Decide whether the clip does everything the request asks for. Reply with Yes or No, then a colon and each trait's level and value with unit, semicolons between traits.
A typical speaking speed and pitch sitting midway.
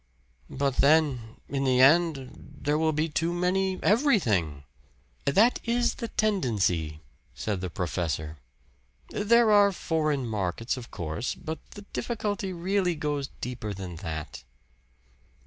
No: slow, 125 wpm; medium, 145 Hz